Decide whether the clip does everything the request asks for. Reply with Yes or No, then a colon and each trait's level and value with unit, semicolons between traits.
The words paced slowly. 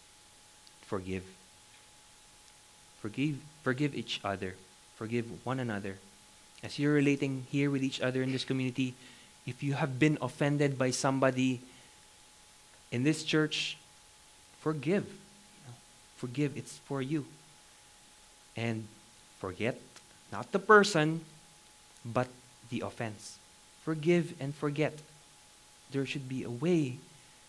Yes: slow, 110 wpm